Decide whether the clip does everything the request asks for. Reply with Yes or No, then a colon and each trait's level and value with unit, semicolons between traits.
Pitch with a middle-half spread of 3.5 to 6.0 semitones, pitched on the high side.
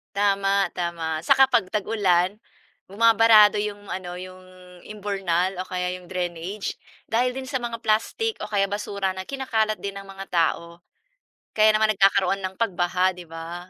No: average, 2.9 semitones; high, 195 Hz